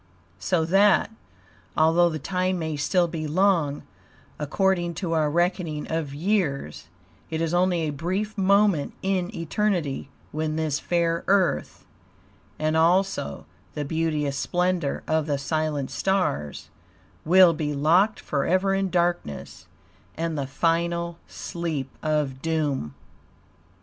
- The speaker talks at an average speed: No, slow, 120 wpm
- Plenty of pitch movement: No, average, 3.4 semitones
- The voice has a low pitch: No, medium, 165 Hz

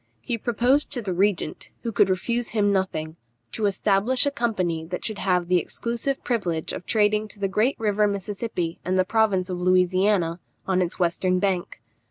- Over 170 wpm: Yes, average, 180 wpm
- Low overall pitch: No, high, 195 Hz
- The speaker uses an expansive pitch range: No, average, 3.3 semitones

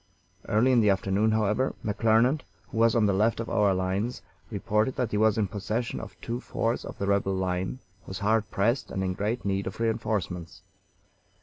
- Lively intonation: No, average, 2.7 semitones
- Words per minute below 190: No, average, 195 wpm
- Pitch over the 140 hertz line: No, low, 105 Hz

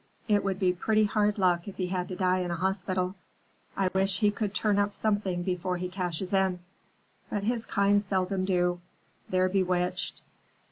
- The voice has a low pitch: No, high, 190 Hz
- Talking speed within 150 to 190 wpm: Yes, average, 180 wpm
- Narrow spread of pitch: Yes, narrow, 1.9 semitones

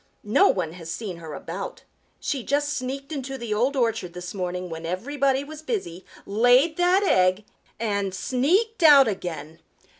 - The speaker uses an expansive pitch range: Yes, wide, 7.7 semitones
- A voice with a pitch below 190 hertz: No, high, 230 Hz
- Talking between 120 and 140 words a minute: No, average, 155 wpm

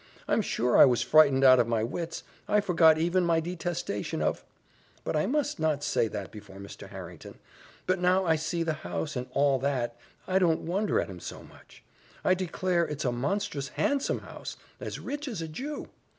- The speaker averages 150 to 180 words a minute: No, average, 195 wpm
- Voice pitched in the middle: Yes, medium, 160 Hz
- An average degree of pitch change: No, wide, 6.1 semitones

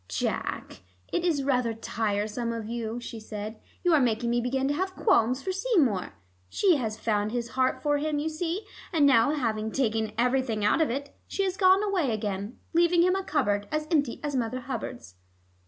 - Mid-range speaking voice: No, very high, 255 Hz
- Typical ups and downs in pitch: No, wide, 5.8 semitones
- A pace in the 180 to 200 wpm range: Yes, average, 190 wpm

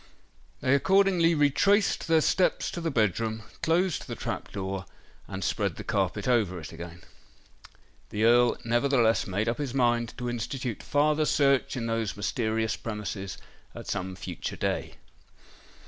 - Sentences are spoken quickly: No, average, 145 wpm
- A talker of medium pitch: No, low, 120 Hz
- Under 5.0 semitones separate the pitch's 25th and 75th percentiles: No, wide, 5.4 semitones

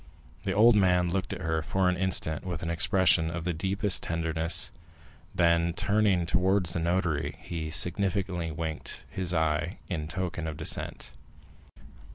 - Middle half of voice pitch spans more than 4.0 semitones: No, narrow, 2.5 semitones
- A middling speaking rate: Yes, average, 150 wpm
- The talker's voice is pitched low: Yes, very low, 85 Hz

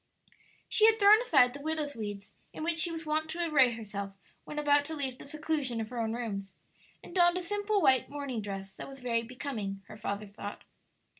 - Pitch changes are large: Yes, wide, 6.6 semitones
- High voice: Yes, very high, 270 Hz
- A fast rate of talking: Yes, fast, 210 wpm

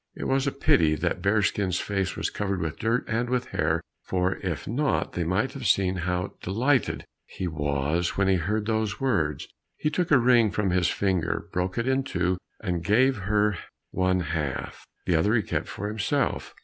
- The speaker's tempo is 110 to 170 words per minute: No, average, 190 wpm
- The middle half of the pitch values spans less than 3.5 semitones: No, average, 4.6 semitones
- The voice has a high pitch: No, low, 100 Hz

